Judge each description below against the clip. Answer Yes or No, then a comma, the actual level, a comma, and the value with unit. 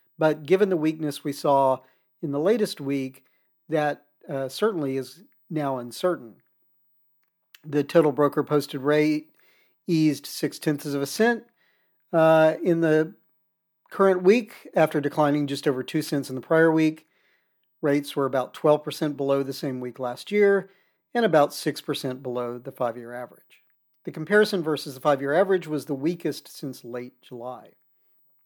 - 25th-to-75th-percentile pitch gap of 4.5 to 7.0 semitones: No, average, 3.4 semitones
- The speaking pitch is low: No, medium, 150 Hz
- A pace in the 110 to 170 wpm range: Yes, average, 155 wpm